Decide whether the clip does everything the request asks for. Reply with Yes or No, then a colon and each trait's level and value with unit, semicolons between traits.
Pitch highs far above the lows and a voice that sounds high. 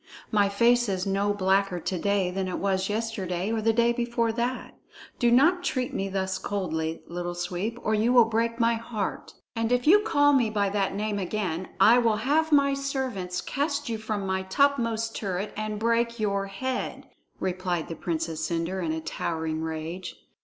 No: average, 4.1 semitones; high, 210 Hz